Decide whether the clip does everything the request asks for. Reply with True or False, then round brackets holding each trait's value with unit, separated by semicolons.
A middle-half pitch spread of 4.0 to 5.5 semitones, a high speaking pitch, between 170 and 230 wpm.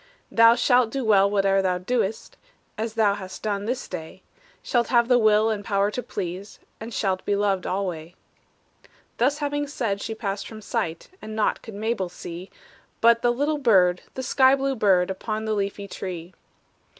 False (3.5 semitones; 210 Hz; 175 wpm)